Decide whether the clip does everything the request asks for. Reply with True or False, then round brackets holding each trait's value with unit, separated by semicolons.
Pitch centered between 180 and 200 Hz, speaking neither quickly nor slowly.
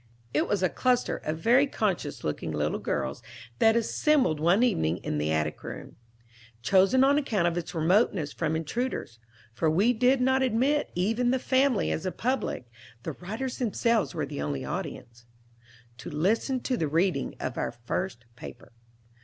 True (190 Hz; 165 wpm)